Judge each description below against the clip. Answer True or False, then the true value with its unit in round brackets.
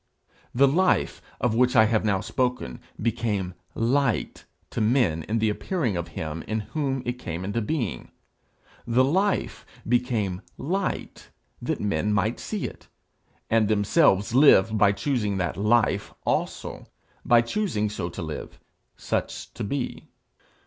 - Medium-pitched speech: False (115 Hz)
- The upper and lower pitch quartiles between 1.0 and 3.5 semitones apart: False (4.1 semitones)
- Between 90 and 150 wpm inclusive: True (140 wpm)